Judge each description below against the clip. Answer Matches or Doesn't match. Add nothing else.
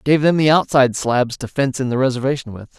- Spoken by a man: Matches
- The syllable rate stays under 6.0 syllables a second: Doesn't match